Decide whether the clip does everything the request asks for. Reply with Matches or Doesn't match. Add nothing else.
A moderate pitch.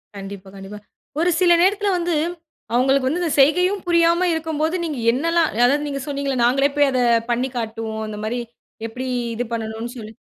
Doesn't match